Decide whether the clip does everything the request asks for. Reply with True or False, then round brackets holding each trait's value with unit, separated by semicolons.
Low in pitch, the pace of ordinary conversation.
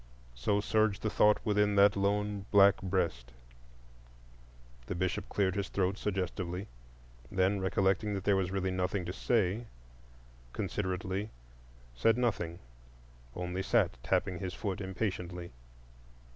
False (95 Hz; 120 wpm)